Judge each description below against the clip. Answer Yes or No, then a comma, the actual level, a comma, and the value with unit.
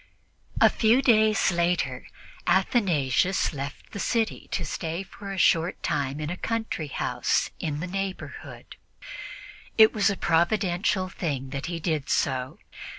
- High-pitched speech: No, medium, 175 Hz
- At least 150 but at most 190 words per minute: No, average, 140 wpm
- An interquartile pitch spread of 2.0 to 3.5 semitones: No, average, 4.8 semitones